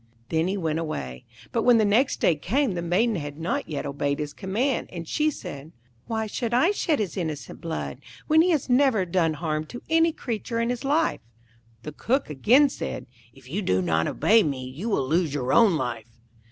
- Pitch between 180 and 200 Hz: Yes, medium, 185 Hz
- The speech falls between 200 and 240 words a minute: Yes, fast, 205 wpm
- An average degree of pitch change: No, wide, 8.2 semitones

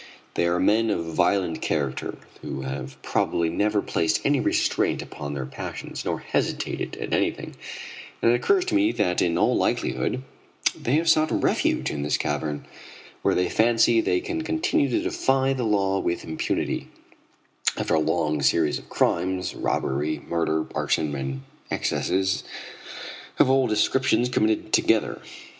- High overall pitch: No, very low, 95 Hz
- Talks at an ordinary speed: Yes, average, 150 wpm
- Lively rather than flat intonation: Yes, wide, 8.9 semitones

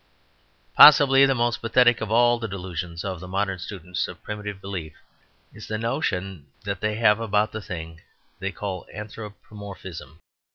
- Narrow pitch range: No, average, 3.4 semitones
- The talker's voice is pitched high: No, low, 100 Hz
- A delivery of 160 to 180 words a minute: No, average, 150 wpm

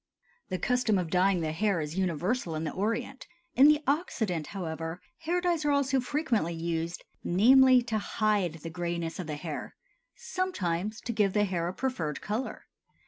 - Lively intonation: Yes, wide, 7.2 semitones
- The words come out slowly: No, average, 170 wpm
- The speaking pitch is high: Yes, high, 195 Hz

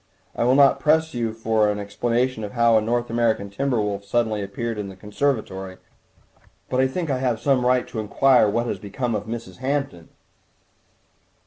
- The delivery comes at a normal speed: Yes, average, 185 wpm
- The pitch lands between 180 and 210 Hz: No, low, 115 Hz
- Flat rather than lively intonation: No, average, 3.6 semitones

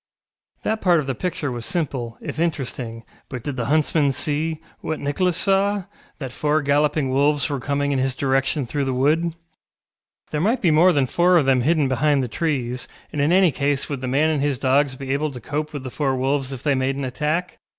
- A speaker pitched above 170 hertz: No, medium, 145 Hz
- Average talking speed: No, fast, 215 wpm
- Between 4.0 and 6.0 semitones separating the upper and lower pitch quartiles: No, average, 2.9 semitones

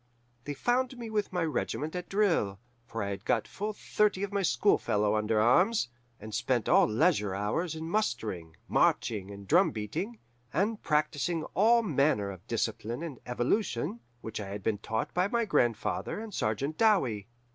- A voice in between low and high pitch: Yes, medium, 145 Hz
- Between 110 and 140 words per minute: No, average, 170 wpm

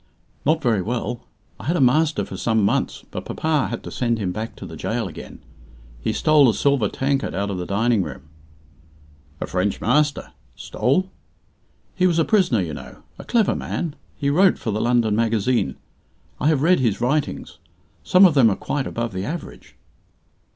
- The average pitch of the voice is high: No, low, 120 Hz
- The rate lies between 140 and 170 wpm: No, average, 185 wpm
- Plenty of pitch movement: Yes, wide, 5.9 semitones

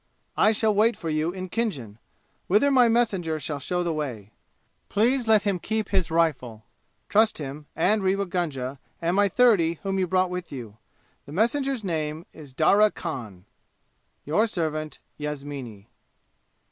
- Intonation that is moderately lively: No, wide, 5.9 semitones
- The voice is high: No, medium, 175 Hz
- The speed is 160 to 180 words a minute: No, average, 150 wpm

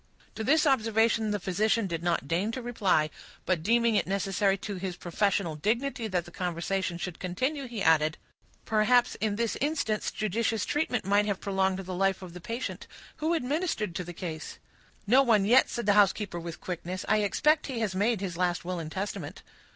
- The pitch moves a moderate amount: Yes, average, 4.3 semitones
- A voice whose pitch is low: No, high, 200 Hz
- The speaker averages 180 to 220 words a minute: Yes, average, 190 wpm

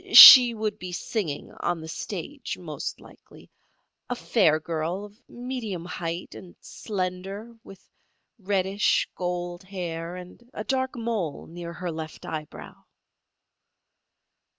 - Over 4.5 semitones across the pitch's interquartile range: No, average, 4.0 semitones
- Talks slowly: Yes, slow, 120 wpm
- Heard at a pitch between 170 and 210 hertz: Yes, medium, 185 Hz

